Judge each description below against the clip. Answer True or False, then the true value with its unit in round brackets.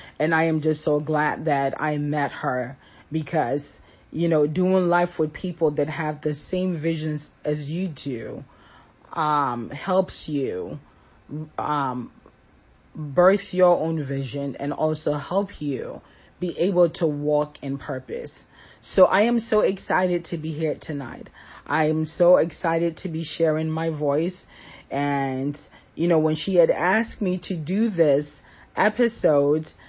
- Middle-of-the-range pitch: True (155 Hz)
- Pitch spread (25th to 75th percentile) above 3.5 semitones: False (3.1 semitones)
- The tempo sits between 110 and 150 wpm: True (145 wpm)